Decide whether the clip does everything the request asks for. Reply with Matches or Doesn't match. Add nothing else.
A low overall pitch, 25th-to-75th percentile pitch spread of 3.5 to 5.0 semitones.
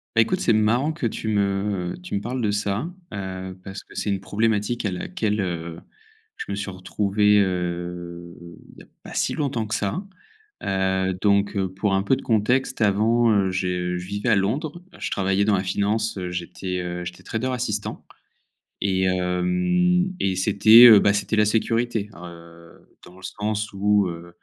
Doesn't match